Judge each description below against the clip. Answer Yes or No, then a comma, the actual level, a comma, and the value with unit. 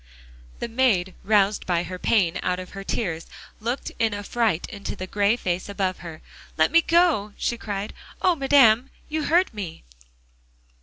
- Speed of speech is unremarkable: Yes, average, 160 wpm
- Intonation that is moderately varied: Yes, average, 4.6 semitones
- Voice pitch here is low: No, high, 205 Hz